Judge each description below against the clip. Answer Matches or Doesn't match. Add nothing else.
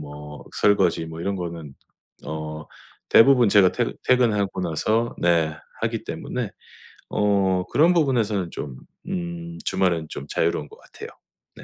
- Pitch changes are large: Matches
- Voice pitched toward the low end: Matches